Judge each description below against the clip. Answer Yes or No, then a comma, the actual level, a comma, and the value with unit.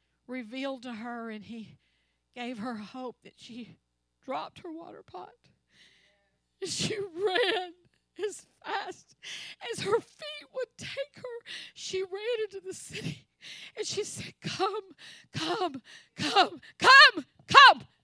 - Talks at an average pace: No, slow, 125 wpm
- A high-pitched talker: Yes, very high, 315 Hz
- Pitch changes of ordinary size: No, wide, 8.9 semitones